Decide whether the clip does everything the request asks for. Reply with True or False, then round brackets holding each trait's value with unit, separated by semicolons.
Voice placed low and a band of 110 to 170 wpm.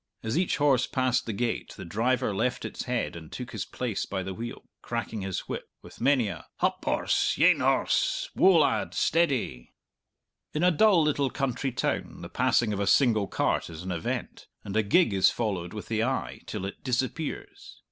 False (120 Hz; 190 wpm)